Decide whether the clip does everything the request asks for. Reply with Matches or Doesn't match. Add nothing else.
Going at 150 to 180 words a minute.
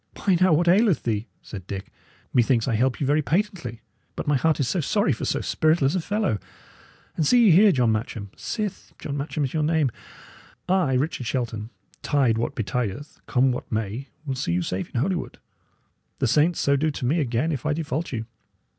Doesn't match